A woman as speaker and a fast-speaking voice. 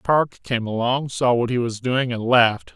No: male; fast, 220 wpm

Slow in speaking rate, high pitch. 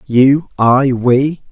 No: slow, 120 wpm; low, 130 Hz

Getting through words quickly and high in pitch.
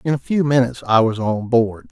No: fast, 250 wpm; low, 125 Hz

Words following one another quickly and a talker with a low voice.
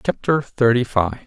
No: average, 140 wpm; low, 120 Hz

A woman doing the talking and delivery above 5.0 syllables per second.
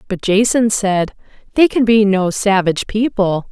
No: female; 4.6 syllables/s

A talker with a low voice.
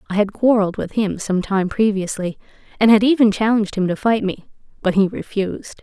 No: high, 205 Hz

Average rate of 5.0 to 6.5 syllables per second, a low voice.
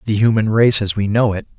Yes: 6.0 syllables/s; low, 110 Hz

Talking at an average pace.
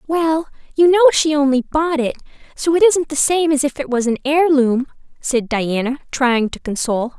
Yes: average, 190 wpm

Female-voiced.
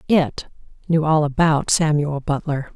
Yes: female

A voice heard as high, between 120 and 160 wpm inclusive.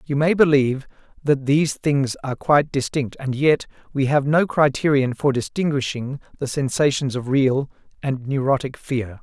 No: medium, 140 Hz; average, 155 wpm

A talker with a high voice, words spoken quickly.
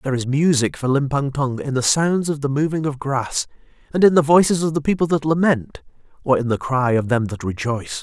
No: medium, 140 Hz; fast, 230 wpm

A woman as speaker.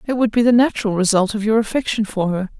Yes: female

